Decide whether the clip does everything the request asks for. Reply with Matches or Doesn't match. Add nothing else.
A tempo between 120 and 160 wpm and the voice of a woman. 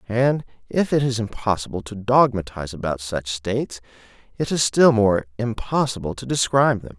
Doesn't match